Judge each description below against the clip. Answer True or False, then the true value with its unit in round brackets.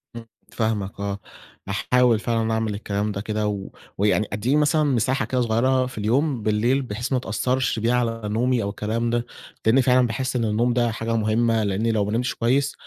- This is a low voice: True (115 Hz)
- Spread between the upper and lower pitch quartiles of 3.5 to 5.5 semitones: False (2.8 semitones)